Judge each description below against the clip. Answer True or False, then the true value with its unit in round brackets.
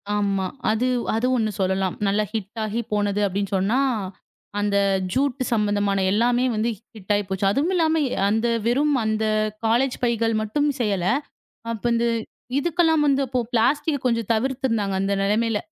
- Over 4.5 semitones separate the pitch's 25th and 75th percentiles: False (3.8 semitones)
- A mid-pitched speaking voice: False (225 Hz)